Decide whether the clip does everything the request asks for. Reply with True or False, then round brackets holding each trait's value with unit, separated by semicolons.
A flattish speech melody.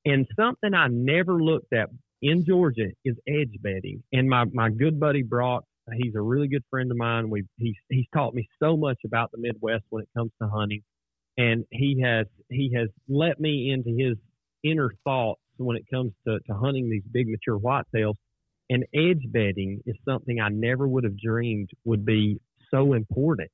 False (3.7 semitones)